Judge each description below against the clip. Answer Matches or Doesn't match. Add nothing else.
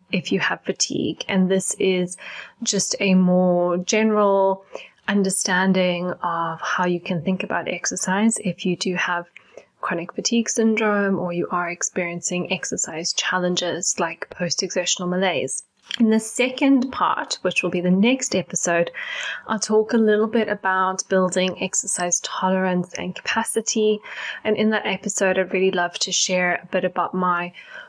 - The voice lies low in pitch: Doesn't match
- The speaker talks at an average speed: Matches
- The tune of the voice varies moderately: Matches